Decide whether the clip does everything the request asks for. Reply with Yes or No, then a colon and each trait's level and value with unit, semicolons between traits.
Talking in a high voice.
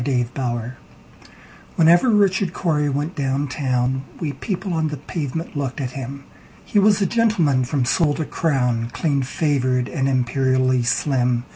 No: medium, 140 Hz